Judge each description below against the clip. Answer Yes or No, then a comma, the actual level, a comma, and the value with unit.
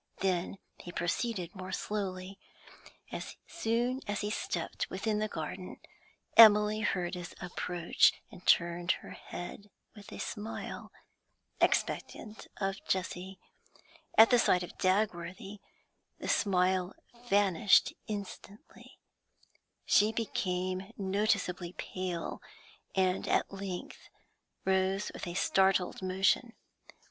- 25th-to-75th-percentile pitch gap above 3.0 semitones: No, narrow, 2.4 semitones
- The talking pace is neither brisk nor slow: No, slow, 105 wpm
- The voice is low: No, high, 190 Hz